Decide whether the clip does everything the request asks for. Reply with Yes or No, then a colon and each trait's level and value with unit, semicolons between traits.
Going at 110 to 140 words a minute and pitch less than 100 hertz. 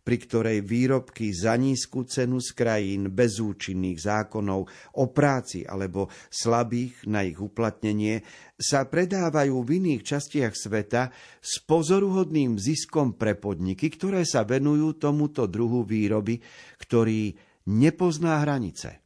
No: average, 120 wpm; low, 120 Hz